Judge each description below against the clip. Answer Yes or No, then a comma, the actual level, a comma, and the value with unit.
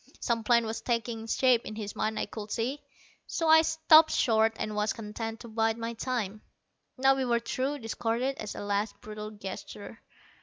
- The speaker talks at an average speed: Yes, average, 185 wpm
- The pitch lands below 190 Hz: No, high, 225 Hz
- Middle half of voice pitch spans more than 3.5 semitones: No, average, 2.8 semitones